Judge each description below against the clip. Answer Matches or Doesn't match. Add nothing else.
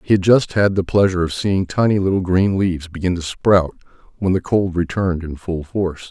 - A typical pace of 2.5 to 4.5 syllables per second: Doesn't match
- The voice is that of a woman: Doesn't match